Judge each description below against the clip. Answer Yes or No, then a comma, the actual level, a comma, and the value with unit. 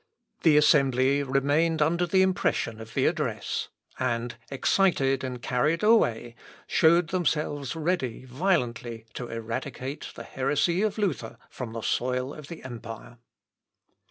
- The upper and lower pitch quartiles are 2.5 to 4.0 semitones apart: No, average, 5.3 semitones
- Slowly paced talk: Yes, slow, 130 wpm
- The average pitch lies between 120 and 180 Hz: Yes, low, 135 Hz